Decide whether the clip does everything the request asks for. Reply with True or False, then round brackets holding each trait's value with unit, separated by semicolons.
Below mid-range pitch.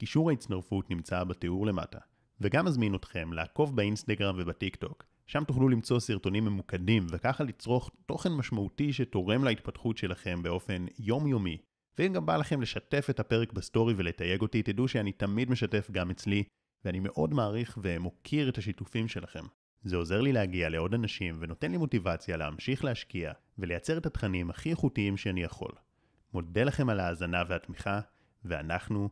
True (105 Hz)